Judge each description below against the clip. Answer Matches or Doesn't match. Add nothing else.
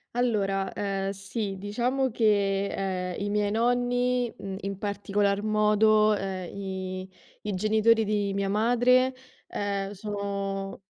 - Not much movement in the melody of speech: Matches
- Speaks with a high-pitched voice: Matches